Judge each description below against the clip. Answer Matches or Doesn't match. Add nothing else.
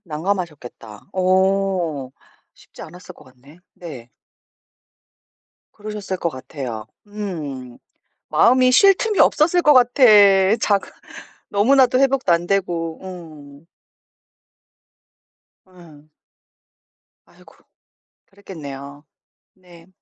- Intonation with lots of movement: Matches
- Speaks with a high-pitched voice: Doesn't match